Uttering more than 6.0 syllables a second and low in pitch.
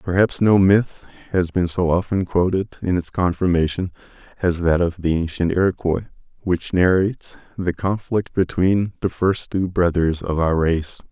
No: 4.6 syllables/s; very low, 90 Hz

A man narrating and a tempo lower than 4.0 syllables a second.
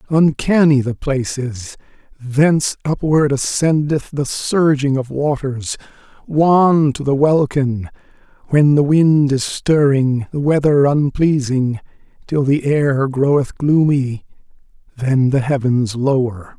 Yes: male; 3.7 syllables/s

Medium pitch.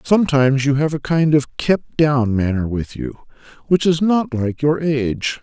Yes: medium, 145 Hz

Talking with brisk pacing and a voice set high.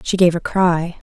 No: fast, 215 wpm; medium, 175 Hz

